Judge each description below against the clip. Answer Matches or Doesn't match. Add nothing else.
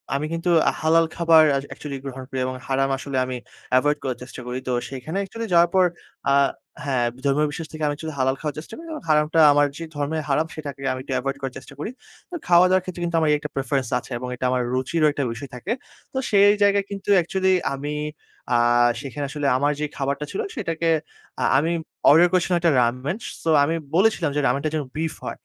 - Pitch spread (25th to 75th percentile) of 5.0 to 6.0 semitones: Doesn't match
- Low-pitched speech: Doesn't match